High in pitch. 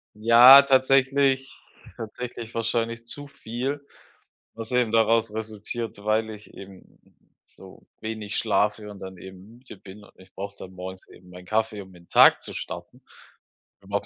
No: low, 110 Hz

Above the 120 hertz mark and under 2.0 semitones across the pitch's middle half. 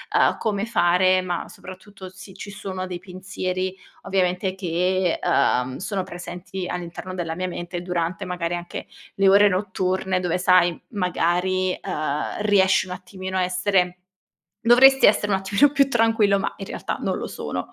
Yes: medium, 185 Hz; narrow, 1.5 semitones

